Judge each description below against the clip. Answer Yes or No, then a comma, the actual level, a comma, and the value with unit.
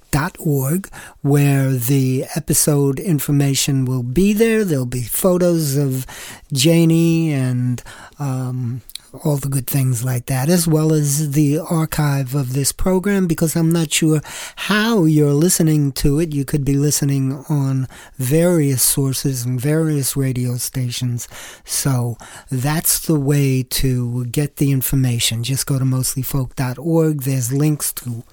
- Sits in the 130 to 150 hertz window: Yes, medium, 140 Hz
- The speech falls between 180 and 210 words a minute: No, average, 140 wpm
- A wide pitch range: No, average, 3.3 semitones